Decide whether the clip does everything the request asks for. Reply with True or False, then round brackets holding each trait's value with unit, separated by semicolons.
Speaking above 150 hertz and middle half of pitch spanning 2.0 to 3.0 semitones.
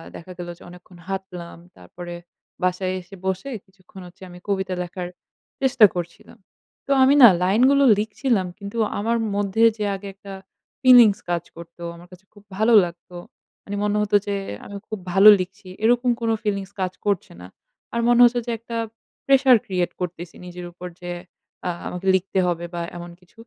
False (190 Hz; 3.5 semitones)